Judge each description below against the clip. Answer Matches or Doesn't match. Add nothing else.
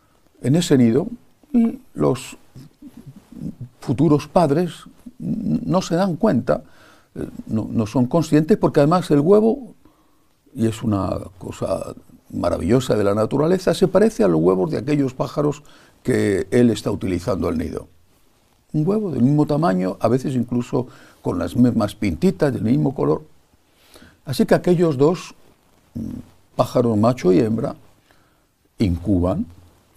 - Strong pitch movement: Matches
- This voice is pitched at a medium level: Matches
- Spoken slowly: Matches